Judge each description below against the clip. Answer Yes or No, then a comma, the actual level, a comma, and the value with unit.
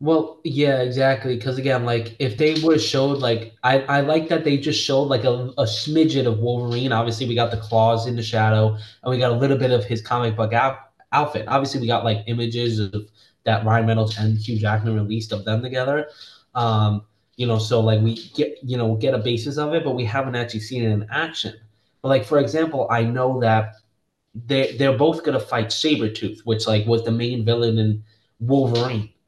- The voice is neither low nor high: No, low, 120 Hz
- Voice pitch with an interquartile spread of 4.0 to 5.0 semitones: No, average, 3.3 semitones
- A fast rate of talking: Yes, fast, 215 wpm